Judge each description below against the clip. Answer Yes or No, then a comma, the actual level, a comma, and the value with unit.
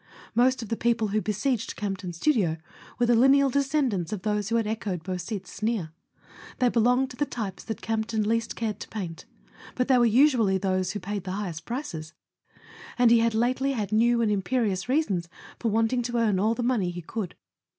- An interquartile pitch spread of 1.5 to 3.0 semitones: No, average, 3.9 semitones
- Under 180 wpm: No, average, 200 wpm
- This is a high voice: Yes, high, 220 Hz